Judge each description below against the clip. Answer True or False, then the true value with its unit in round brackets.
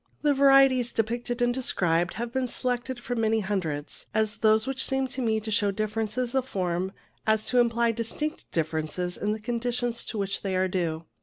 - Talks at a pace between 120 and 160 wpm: False (190 wpm)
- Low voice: False (225 Hz)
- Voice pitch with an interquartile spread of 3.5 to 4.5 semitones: True (4.0 semitones)